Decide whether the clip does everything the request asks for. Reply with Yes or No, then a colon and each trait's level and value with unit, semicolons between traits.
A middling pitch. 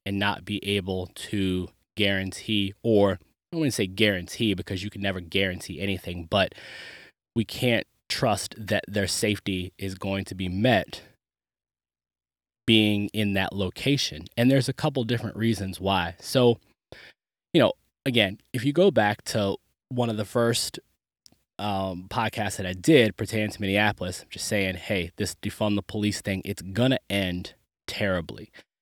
No: low, 100 Hz